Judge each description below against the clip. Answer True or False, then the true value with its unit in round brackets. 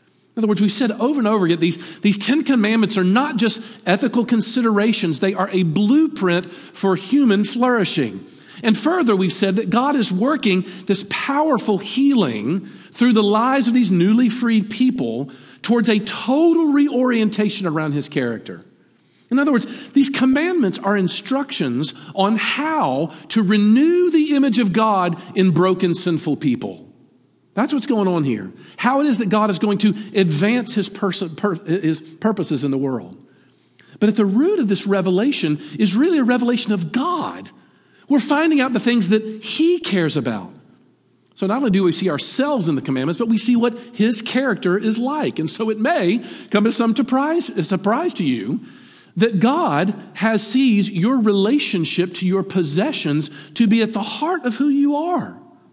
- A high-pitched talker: True (215 Hz)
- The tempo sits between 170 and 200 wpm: True (175 wpm)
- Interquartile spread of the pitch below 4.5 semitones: False (5.5 semitones)